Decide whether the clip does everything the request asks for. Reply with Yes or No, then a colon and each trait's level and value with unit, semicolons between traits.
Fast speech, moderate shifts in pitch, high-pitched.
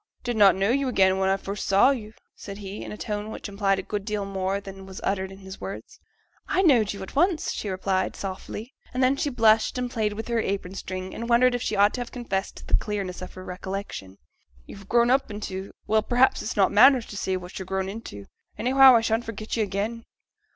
Yes: fast, 235 wpm; average, 3.4 semitones; high, 205 Hz